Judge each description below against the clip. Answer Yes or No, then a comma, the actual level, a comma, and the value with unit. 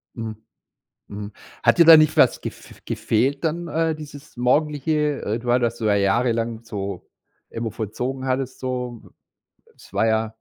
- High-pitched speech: No, low, 125 Hz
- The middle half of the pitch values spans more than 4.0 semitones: Yes, average, 4.6 semitones